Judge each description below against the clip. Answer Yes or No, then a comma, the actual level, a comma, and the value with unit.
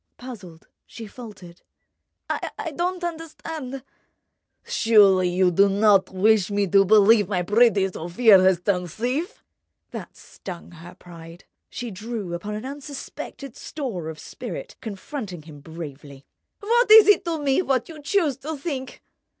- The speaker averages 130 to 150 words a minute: Yes, slow, 135 wpm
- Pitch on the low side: No, high, 215 Hz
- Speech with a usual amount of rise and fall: No, wide, 7.4 semitones